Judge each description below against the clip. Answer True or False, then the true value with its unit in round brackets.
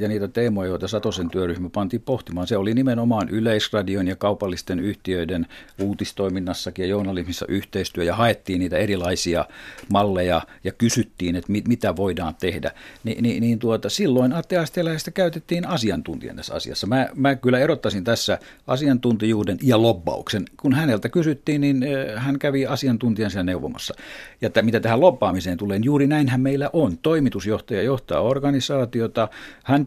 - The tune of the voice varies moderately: False (5.7 semitones)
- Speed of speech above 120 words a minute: True (145 wpm)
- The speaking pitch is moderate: False (110 Hz)